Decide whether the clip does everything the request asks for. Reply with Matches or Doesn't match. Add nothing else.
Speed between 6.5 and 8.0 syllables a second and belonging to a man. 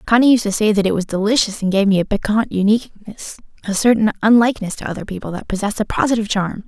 Doesn't match